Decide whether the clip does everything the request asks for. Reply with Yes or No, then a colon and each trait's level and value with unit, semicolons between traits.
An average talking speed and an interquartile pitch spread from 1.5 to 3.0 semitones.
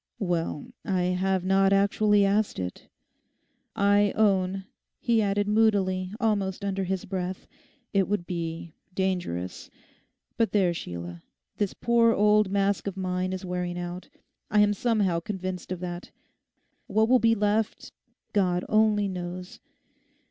No: slow, 130 wpm; narrow, 2.4 semitones